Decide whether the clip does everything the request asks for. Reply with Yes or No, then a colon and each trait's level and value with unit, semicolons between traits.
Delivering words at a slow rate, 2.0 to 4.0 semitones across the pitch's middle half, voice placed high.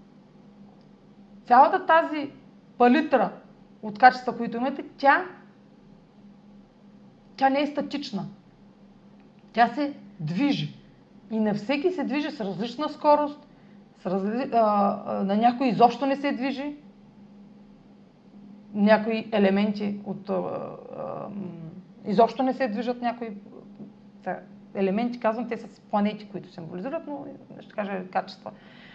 Yes: slow, 105 wpm; average, 3.7 semitones; high, 210 Hz